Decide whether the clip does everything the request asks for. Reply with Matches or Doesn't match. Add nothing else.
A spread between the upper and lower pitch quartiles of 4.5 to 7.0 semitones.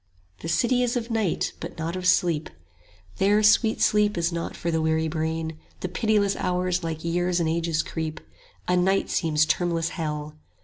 Doesn't match